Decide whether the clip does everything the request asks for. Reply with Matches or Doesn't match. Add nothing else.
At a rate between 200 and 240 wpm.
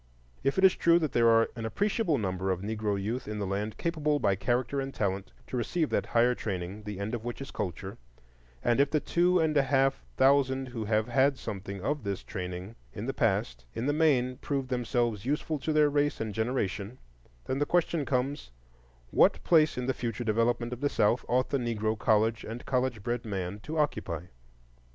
Matches